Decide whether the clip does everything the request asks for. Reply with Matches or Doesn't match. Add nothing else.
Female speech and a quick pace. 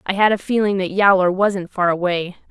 Matches